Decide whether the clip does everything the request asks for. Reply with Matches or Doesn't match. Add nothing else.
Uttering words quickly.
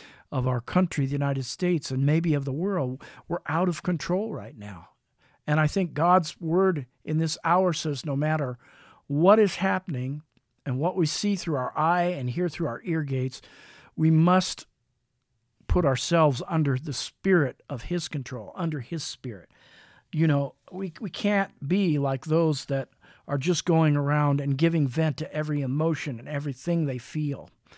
Doesn't match